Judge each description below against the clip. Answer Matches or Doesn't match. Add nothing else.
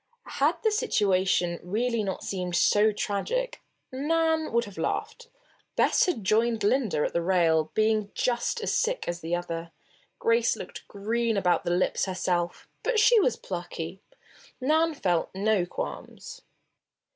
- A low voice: Doesn't match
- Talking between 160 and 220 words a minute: Doesn't match